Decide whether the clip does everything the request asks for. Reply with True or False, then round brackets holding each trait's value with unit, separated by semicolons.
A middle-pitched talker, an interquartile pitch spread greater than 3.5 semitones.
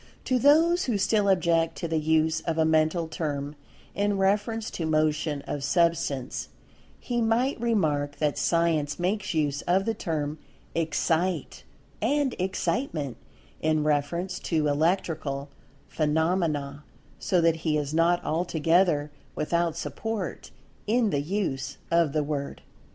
True (165 Hz; 4.1 semitones)